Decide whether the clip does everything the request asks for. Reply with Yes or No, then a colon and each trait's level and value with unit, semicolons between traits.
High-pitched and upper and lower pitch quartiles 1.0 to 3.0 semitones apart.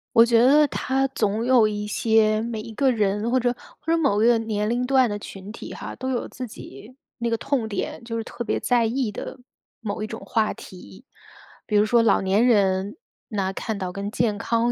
Yes: high, 225 Hz; average, 2.7 semitones